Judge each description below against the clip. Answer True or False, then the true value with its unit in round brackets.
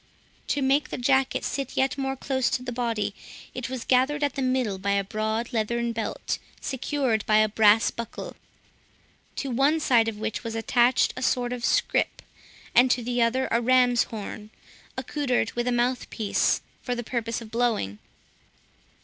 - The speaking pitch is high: True (240 Hz)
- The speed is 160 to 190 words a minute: True (170 wpm)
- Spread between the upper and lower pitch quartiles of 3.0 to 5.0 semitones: False (2.5 semitones)